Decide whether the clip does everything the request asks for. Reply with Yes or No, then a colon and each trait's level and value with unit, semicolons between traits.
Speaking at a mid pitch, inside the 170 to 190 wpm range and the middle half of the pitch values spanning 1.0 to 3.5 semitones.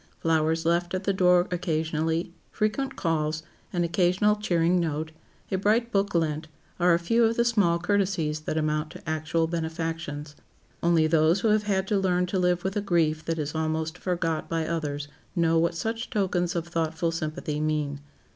Yes: medium, 170 Hz; average, 175 wpm; average, 2.8 semitones